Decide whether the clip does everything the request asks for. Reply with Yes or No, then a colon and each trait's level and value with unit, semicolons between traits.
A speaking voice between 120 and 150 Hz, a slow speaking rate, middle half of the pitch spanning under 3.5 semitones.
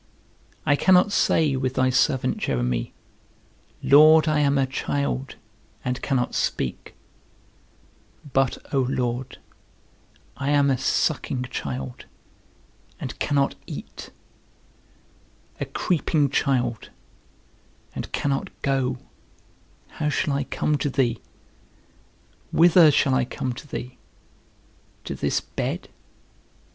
Yes: low, 135 Hz; slow, 105 wpm; average, 2.7 semitones